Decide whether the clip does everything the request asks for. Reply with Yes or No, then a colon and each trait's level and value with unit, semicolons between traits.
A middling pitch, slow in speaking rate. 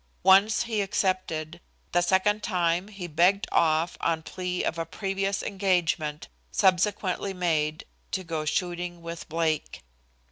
Yes: medium, 180 Hz; slow, 130 wpm